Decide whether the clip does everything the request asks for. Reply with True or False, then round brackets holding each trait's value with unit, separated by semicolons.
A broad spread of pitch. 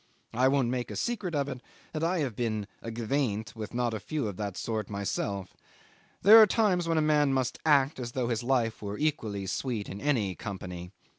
True (5.7 semitones)